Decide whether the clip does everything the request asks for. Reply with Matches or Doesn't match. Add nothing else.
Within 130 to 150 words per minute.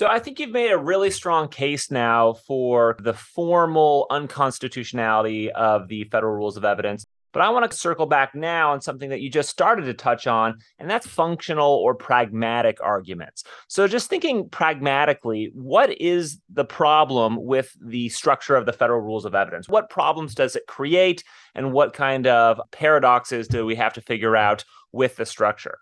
Doesn't match